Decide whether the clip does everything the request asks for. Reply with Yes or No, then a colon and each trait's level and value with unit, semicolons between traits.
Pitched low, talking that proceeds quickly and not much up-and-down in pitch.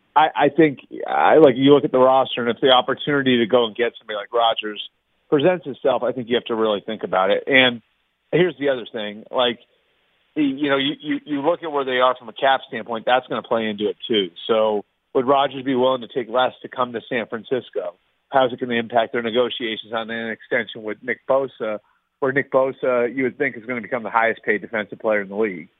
No: low, 125 Hz; fast, 240 wpm; average, 3.2 semitones